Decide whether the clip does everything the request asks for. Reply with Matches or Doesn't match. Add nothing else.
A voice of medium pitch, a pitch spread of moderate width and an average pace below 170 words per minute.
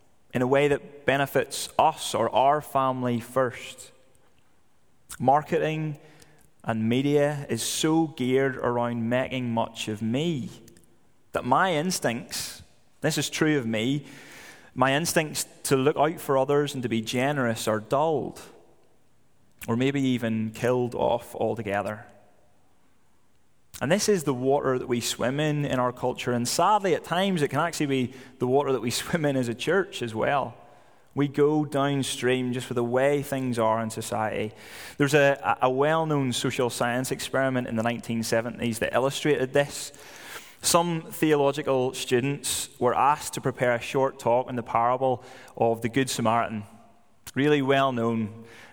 Doesn't match